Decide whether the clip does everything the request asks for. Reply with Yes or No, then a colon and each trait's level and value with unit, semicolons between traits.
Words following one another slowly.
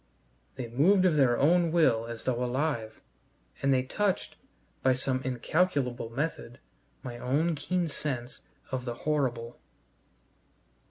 Yes: slow, 125 wpm